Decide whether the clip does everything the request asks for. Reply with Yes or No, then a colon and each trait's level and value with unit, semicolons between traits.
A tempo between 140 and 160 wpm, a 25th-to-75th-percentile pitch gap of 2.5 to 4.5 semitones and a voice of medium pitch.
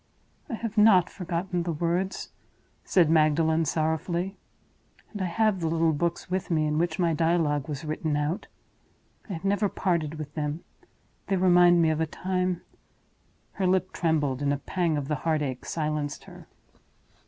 No: average, 170 wpm; average, 2.9 semitones; medium, 165 Hz